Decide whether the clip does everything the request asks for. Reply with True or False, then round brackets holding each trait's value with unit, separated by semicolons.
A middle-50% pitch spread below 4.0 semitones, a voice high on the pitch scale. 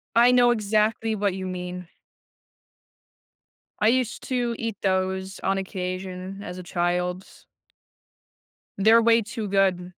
True (3.6 semitones; 195 Hz)